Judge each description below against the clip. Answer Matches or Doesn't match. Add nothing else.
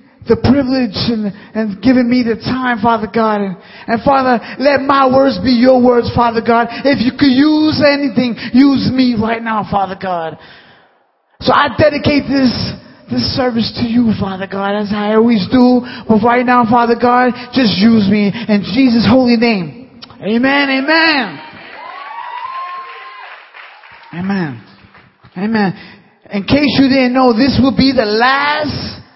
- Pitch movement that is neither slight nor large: Matches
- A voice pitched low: Doesn't match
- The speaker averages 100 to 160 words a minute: Matches